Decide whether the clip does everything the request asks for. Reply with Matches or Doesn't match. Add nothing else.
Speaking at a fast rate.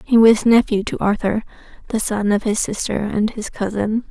Doesn't match